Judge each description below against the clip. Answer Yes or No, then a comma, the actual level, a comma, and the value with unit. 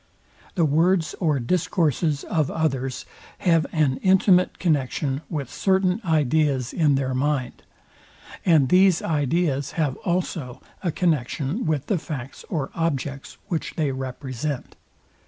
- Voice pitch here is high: No, medium, 155 Hz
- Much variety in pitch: No, average, 4.1 semitones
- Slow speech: Yes, slow, 120 wpm